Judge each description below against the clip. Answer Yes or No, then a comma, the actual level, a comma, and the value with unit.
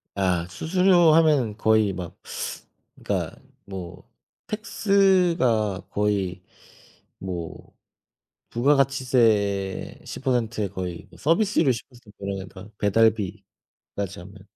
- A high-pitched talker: No, low, 110 Hz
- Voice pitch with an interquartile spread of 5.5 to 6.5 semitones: Yes, wide, 6.2 semitones